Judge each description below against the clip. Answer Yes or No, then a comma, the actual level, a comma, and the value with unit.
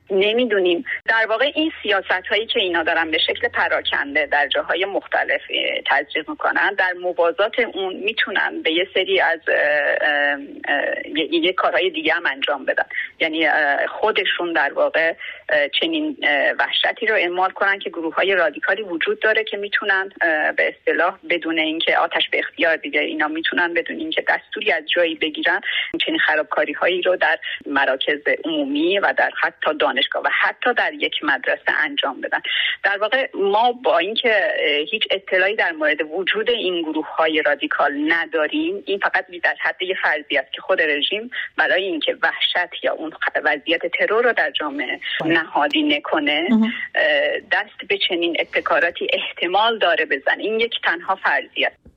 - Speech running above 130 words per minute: Yes, average, 150 wpm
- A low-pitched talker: No, high, 245 Hz